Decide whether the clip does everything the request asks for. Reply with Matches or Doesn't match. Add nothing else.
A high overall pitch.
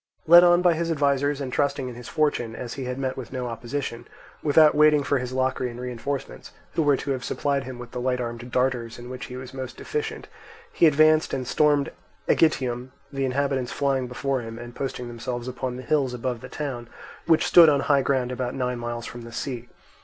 Doesn't match